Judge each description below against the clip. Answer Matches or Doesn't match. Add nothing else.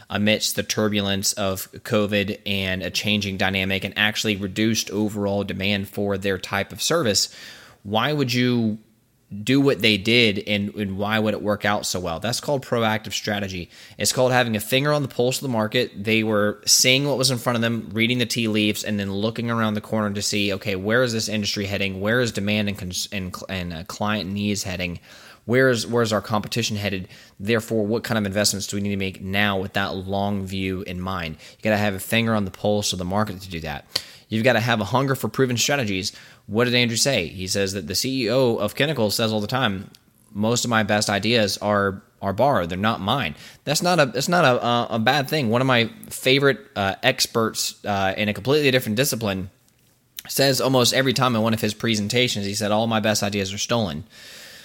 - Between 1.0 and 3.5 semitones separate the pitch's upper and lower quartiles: Matches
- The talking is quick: Matches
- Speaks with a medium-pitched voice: Doesn't match